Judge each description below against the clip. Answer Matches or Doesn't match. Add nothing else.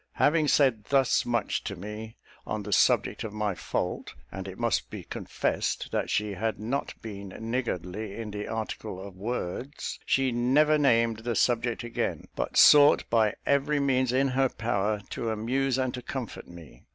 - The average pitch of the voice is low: Matches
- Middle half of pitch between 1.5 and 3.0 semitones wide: Doesn't match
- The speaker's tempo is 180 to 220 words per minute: Doesn't match